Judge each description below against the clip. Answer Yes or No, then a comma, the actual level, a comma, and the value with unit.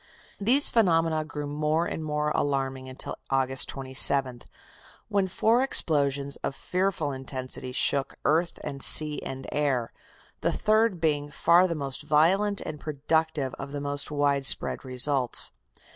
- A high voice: No, medium, 145 Hz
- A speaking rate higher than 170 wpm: No, slow, 135 wpm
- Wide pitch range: No, average, 3.2 semitones